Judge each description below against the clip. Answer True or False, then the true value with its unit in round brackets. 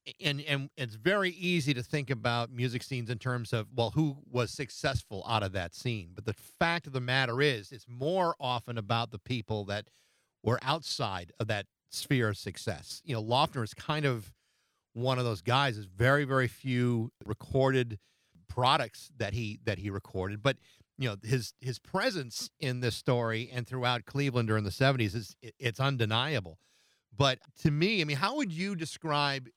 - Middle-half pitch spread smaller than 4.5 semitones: True (3.7 semitones)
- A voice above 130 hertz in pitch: False (125 Hz)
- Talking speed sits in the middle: True (185 wpm)